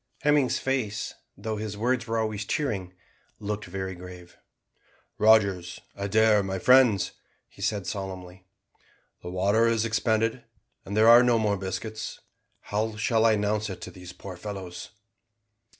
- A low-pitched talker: Yes, low, 105 Hz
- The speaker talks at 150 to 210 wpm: No, average, 140 wpm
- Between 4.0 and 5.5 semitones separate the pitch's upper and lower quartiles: No, average, 2.8 semitones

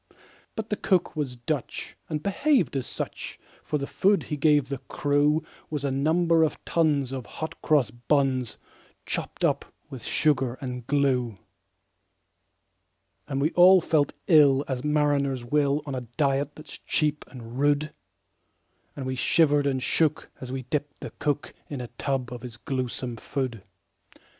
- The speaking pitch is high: No, medium, 140 Hz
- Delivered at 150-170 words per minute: Yes, average, 155 wpm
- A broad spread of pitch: No, average, 2.8 semitones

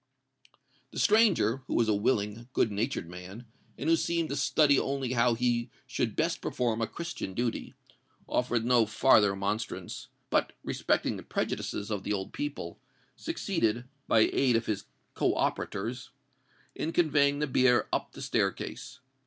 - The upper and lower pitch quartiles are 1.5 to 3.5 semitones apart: No, average, 4.4 semitones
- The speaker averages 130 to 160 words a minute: Yes, average, 155 wpm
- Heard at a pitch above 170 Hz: No, low, 120 Hz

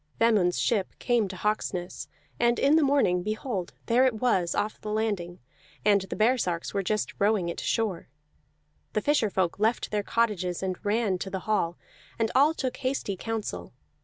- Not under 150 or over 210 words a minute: Yes, average, 175 wpm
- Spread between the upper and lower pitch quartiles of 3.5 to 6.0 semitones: Yes, average, 3.9 semitones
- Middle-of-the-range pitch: No, high, 210 Hz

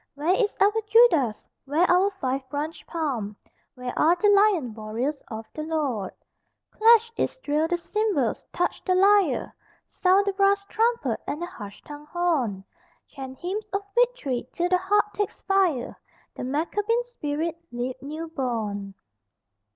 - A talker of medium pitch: No, very high, 330 Hz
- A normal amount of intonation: No, wide, 7.3 semitones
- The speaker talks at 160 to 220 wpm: No, average, 145 wpm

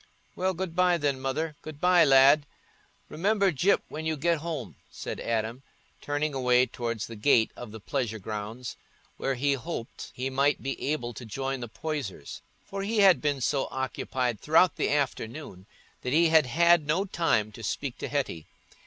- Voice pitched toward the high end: No, medium, 140 Hz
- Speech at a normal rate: Yes, average, 170 wpm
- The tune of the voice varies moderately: Yes, average, 4.8 semitones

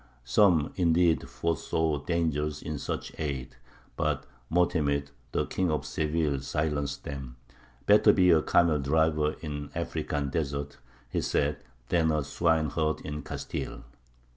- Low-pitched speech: Yes, very low, 75 Hz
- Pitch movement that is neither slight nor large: No, narrow, 2.3 semitones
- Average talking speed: No, slow, 125 wpm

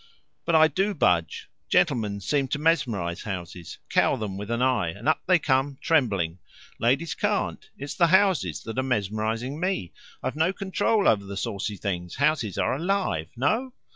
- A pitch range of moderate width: No, wide, 8.4 semitones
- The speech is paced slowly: No, average, 170 wpm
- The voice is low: Yes, low, 125 Hz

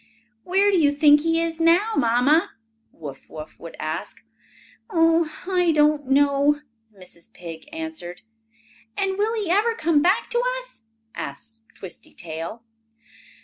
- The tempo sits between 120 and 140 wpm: Yes, slow, 135 wpm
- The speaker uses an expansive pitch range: Yes, wide, 8.0 semitones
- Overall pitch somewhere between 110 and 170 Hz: No, very high, 300 Hz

